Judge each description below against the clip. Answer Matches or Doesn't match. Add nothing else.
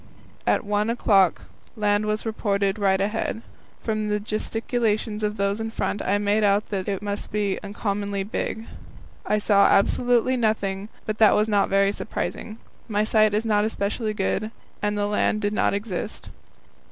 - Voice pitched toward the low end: Doesn't match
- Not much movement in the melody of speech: Matches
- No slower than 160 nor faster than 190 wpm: Matches